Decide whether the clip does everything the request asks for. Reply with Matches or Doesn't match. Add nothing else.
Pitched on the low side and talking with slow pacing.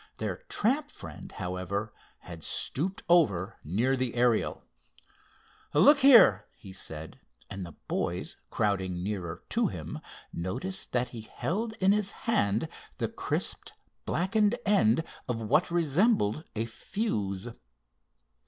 Matches